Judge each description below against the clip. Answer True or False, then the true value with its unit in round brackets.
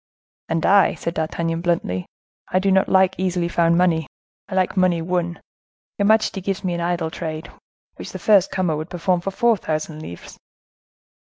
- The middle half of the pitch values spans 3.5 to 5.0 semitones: False (2.4 semitones)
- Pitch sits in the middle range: True (175 Hz)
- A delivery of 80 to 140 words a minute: False (175 wpm)